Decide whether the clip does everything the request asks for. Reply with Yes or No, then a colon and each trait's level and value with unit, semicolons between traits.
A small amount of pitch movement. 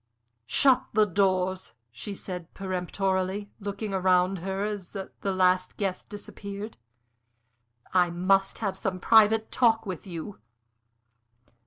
Yes: narrow, 1.9 semitones